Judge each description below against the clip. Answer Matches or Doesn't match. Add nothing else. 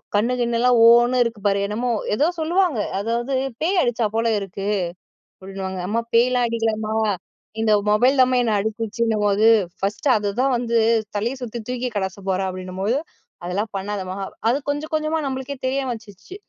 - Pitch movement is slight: Doesn't match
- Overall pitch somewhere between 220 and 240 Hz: Matches